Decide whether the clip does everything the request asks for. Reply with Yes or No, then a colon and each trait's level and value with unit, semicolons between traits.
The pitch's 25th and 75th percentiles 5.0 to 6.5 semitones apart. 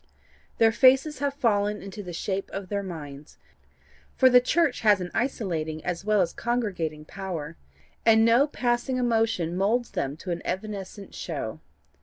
Yes: average, 5.3 semitones